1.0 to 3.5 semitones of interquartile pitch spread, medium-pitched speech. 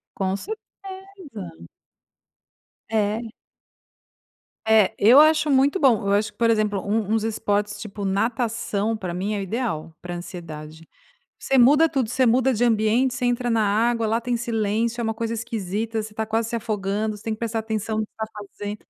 No: narrow, 2.6 semitones; high, 220 Hz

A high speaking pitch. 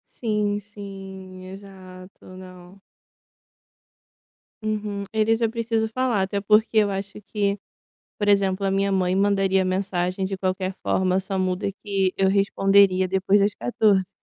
Yes: high, 195 Hz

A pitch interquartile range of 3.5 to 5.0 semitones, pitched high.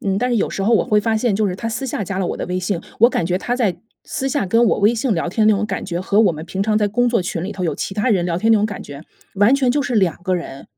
Yes: average, 4.0 semitones; high, 205 Hz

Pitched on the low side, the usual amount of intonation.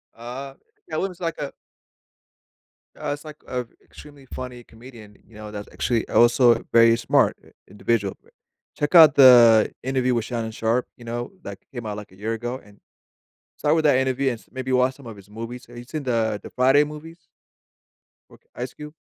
Yes: low, 120 Hz; average, 3.1 semitones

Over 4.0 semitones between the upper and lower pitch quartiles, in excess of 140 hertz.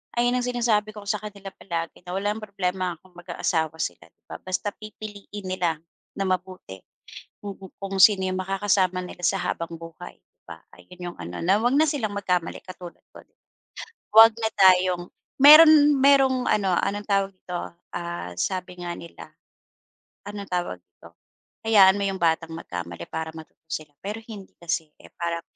No: average, 3.2 semitones; high, 190 Hz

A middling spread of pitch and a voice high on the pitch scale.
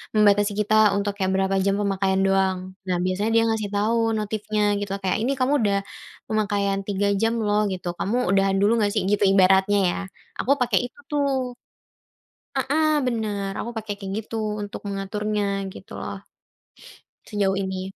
No: narrow, 1.9 semitones; high, 205 Hz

